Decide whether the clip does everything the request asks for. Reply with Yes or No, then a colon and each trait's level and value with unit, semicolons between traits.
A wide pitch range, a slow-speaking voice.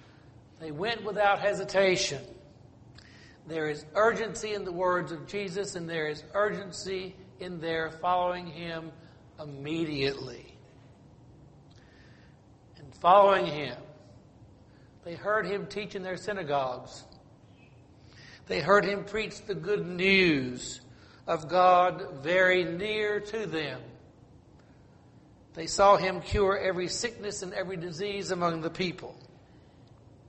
Yes: wide, 5.9 semitones; slow, 110 wpm